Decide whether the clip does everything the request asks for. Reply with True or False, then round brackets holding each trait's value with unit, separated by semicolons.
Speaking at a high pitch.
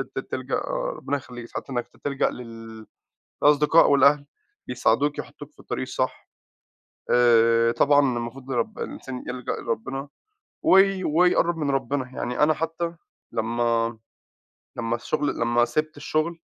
False (135 Hz)